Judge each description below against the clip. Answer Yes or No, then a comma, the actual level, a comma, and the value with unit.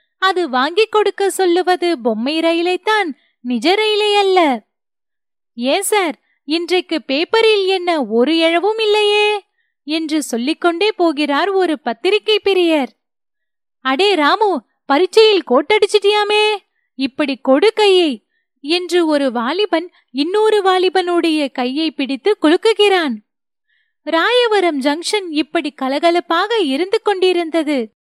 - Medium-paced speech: Yes, average, 95 wpm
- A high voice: Yes, very high, 345 Hz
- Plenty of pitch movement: Yes, wide, 6.0 semitones